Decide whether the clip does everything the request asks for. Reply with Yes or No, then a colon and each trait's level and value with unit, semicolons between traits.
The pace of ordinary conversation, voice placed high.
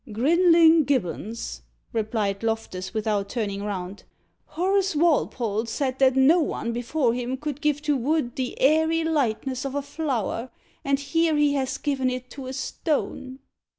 Yes: average, 150 wpm; very high, 265 Hz